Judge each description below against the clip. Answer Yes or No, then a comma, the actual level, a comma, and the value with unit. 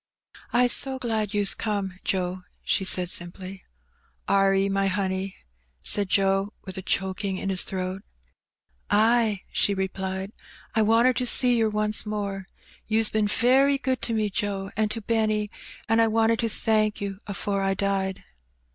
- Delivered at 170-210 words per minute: No, average, 160 wpm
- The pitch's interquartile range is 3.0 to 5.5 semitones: No, narrow, 2.4 semitones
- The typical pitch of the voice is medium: No, high, 205 Hz